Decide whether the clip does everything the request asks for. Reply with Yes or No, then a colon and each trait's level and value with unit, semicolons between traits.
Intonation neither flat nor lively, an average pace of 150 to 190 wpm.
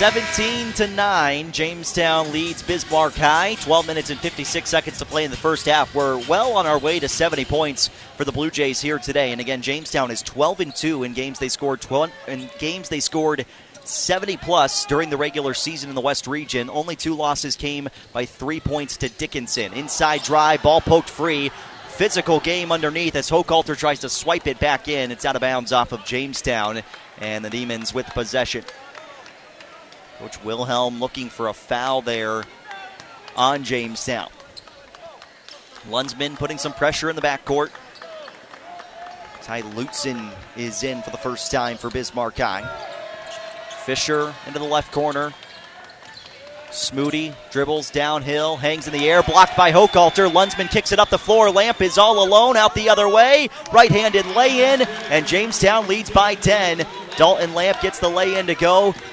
Yes: average, 5.0 semitones; average, 165 wpm